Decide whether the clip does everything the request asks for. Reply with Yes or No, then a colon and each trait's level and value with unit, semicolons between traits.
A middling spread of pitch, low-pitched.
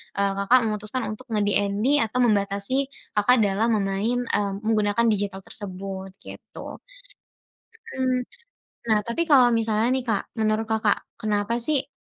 No: average, 3.0 semitones; high, 215 Hz